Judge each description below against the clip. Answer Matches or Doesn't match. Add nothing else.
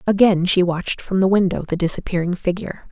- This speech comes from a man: Doesn't match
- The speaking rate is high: Doesn't match